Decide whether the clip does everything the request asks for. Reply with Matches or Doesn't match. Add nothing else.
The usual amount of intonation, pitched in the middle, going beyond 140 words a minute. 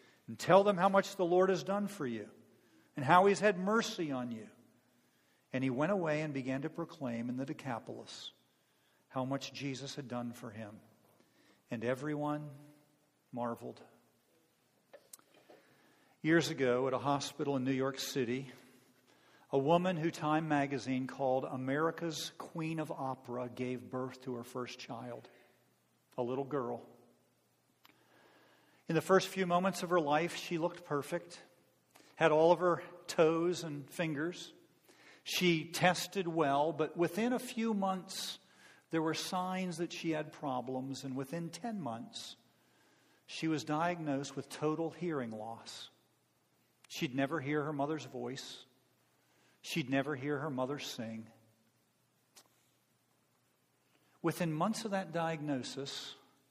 Doesn't match